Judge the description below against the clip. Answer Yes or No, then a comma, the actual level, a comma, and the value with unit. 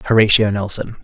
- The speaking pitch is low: Yes, low, 105 Hz